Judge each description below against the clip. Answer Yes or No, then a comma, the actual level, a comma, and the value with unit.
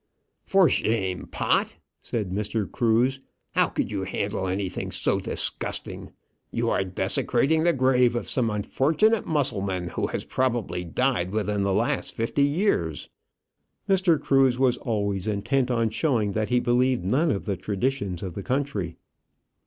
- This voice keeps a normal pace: Yes, average, 145 wpm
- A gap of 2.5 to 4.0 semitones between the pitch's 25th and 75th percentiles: No, average, 5.3 semitones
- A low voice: Yes, low, 115 Hz